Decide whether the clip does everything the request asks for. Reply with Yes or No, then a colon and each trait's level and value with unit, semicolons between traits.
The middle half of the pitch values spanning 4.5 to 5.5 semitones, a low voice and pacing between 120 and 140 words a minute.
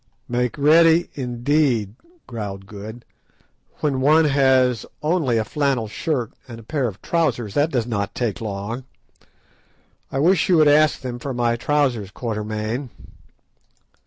Yes: average, 4.8 semitones; low, 125 Hz; slow, 135 wpm